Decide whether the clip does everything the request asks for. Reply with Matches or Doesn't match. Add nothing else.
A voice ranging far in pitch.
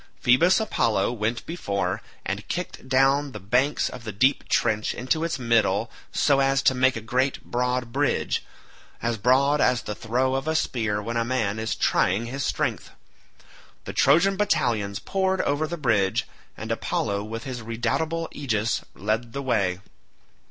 Doesn't match